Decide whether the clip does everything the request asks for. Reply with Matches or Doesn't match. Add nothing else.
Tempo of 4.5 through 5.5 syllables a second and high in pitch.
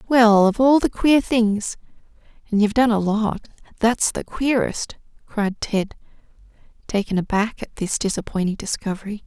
Matches